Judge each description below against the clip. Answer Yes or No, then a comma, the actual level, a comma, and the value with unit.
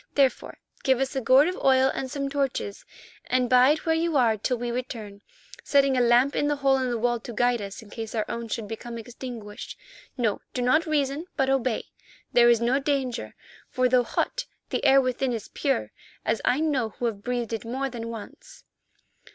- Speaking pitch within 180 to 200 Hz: No, very high, 250 Hz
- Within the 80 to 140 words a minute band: No, average, 200 wpm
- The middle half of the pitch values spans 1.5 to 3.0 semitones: Yes, narrow, 2.6 semitones